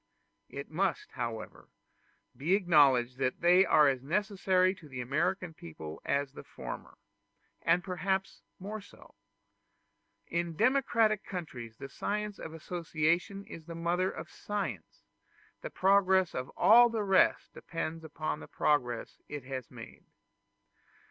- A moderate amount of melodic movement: No, wide, 5.8 semitones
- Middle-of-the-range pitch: Yes, medium, 170 Hz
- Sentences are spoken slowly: Yes, slow, 130 wpm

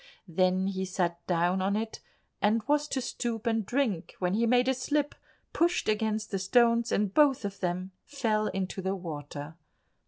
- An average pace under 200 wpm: Yes, average, 175 wpm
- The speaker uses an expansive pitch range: No, average, 4.2 semitones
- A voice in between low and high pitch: No, high, 210 Hz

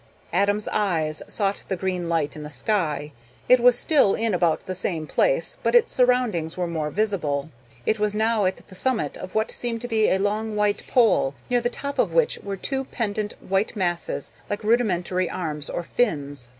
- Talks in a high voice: Yes, high, 200 Hz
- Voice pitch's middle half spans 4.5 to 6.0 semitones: Yes, average, 4.9 semitones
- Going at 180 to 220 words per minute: Yes, average, 190 wpm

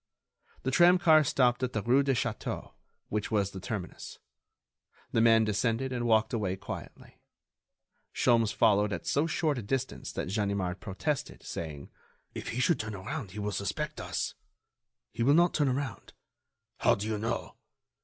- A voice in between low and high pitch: No, low, 115 Hz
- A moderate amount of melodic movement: Yes, average, 4.5 semitones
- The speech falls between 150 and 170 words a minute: Yes, average, 160 wpm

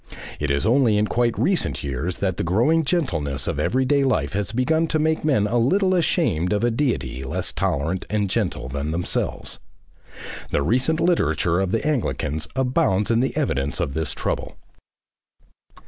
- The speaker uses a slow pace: No, average, 165 wpm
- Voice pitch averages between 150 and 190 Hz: No, low, 105 Hz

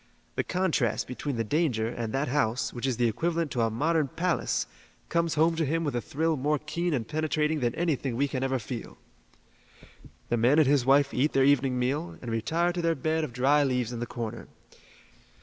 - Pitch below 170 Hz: Yes, medium, 140 Hz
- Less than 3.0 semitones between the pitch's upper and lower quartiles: No, average, 4.7 semitones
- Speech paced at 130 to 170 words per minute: No, fast, 205 wpm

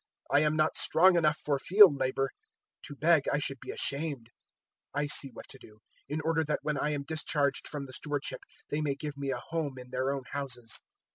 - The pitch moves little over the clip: Yes, narrow, 2.2 semitones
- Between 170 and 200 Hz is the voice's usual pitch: No, medium, 145 Hz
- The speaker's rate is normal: No, fast, 215 wpm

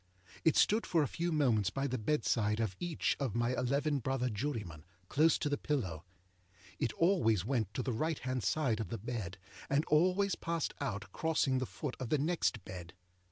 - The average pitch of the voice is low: Yes, low, 130 Hz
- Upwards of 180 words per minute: Yes, average, 190 wpm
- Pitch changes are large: Yes, wide, 5.7 semitones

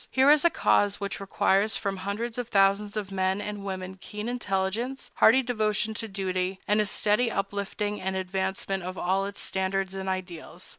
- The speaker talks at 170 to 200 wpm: Yes, average, 180 wpm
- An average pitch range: No, narrow, 1.9 semitones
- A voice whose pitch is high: Yes, high, 200 Hz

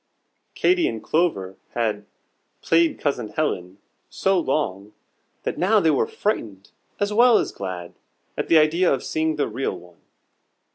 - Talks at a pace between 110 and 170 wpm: Yes, average, 145 wpm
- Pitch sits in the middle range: Yes, medium, 145 Hz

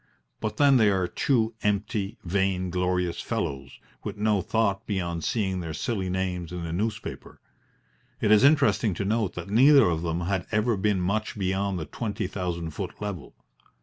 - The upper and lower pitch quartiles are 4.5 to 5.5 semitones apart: No, average, 3.2 semitones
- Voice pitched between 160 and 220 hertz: No, very low, 95 Hz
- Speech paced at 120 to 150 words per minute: No, average, 165 wpm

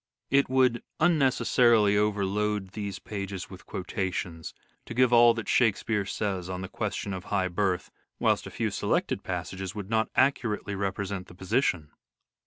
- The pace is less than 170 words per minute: Yes, average, 150 wpm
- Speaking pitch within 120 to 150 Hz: No, low, 100 Hz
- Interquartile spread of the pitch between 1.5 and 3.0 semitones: No, average, 3.5 semitones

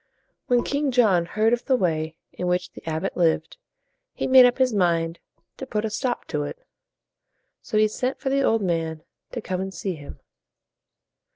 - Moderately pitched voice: No, high, 200 Hz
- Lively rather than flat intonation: Yes, wide, 6.6 semitones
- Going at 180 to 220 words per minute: Yes, average, 185 wpm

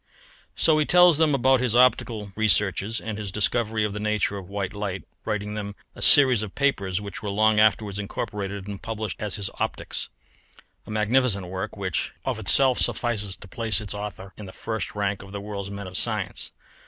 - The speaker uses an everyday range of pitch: No, narrow, 2.0 semitones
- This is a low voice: Yes, low, 105 Hz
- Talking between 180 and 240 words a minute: Yes, average, 190 wpm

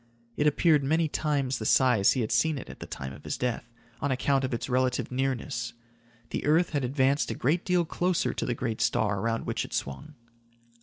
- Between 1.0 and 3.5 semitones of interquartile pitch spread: No, average, 4.0 semitones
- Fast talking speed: Yes, fast, 210 wpm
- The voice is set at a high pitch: No, low, 130 Hz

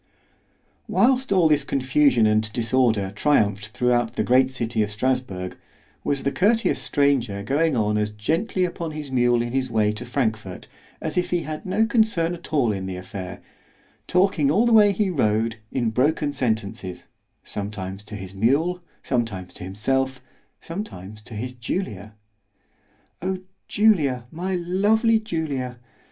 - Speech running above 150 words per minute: No, average, 145 wpm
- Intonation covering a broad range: Yes, wide, 7.6 semitones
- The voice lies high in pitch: No, low, 130 Hz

